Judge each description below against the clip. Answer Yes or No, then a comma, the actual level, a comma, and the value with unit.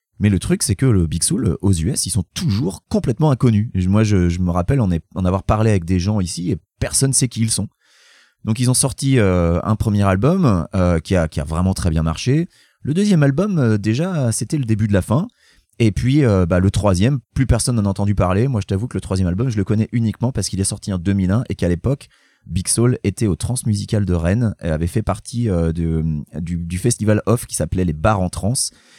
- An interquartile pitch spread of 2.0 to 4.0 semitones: No, average, 4.8 semitones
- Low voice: Yes, low, 105 Hz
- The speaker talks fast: Yes, fast, 245 wpm